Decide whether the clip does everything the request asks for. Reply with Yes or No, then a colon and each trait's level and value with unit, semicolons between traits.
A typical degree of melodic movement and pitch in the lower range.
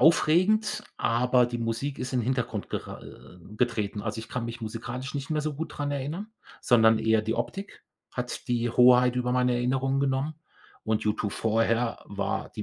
Yes: average, 3.2 semitones; low, 125 Hz